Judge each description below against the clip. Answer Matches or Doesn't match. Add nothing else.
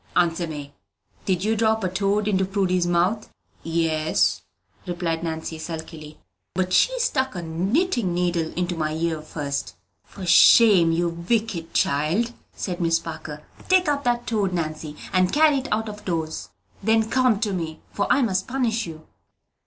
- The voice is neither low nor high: Matches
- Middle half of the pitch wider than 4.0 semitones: Matches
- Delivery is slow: Doesn't match